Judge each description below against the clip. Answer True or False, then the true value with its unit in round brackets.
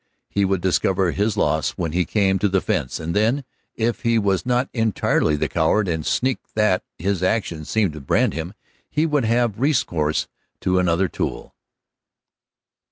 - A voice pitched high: False (95 Hz)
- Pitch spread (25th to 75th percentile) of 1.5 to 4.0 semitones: False (4.9 semitones)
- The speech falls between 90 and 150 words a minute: False (165 wpm)